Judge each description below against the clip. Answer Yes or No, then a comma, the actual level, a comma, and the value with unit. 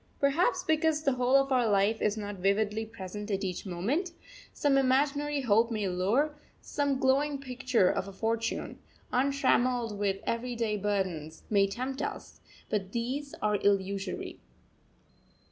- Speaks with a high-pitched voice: Yes, high, 230 Hz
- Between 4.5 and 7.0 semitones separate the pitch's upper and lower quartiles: Yes, average, 5.2 semitones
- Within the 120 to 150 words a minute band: Yes, average, 140 wpm